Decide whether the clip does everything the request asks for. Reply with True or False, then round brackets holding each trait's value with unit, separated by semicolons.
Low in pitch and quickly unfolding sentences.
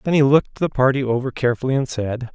True (130 Hz; 230 wpm)